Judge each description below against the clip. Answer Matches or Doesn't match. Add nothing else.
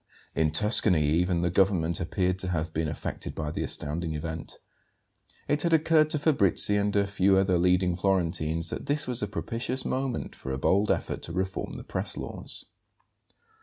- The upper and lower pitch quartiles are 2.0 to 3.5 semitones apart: Doesn't match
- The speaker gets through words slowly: Doesn't match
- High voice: Doesn't match